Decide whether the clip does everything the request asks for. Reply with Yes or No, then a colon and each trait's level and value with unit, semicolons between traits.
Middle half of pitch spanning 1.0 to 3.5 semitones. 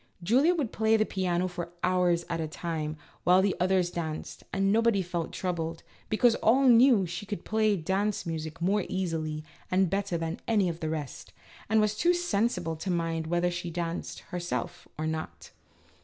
No: average, 4.0 semitones